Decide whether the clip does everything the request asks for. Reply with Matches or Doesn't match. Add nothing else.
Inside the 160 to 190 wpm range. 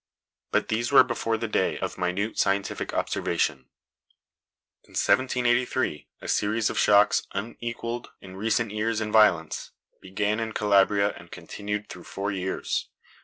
Doesn't match